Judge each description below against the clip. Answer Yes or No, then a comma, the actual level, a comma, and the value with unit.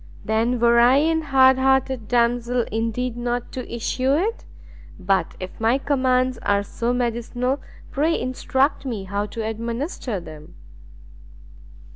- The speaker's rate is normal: No, slow, 130 wpm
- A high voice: Yes, high, 245 Hz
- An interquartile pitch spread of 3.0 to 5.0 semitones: No, narrow, 2.6 semitones